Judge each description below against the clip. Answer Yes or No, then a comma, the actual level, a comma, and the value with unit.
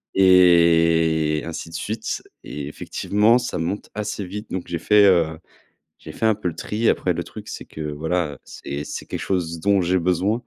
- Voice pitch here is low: Yes, very low, 90 Hz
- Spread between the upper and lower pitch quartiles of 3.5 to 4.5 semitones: Yes, average, 3.8 semitones